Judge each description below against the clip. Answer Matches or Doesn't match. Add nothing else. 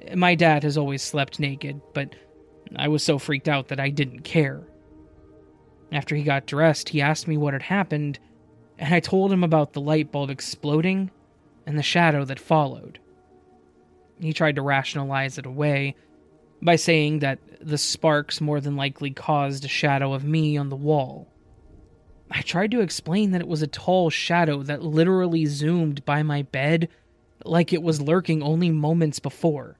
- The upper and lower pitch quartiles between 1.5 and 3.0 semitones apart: Matches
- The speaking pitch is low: Doesn't match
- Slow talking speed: Doesn't match